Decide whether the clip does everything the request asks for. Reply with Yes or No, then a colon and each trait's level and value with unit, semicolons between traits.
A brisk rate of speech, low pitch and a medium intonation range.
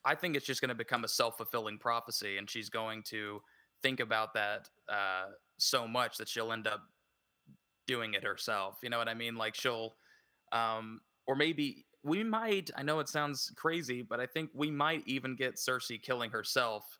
No: average, 195 wpm; low, 120 Hz; average, 4.7 semitones